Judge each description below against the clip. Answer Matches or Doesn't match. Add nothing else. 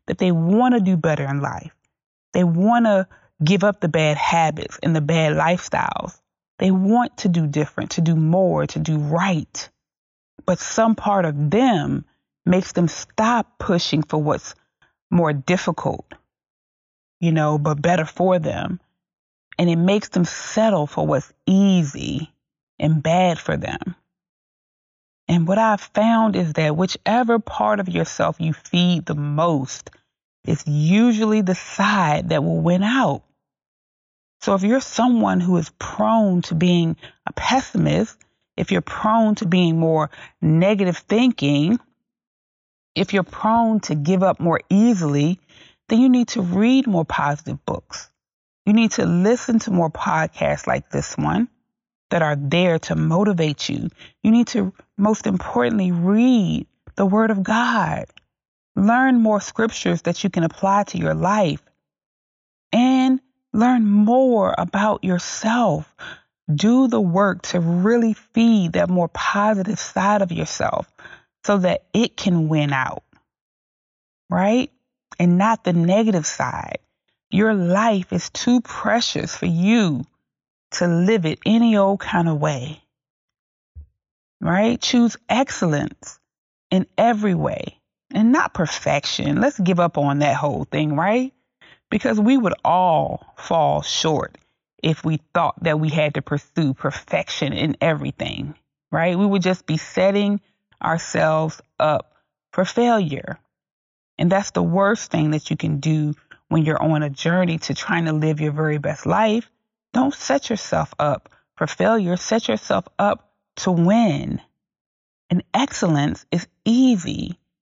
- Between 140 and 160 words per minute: Matches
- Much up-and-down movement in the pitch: Matches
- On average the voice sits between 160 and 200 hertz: Matches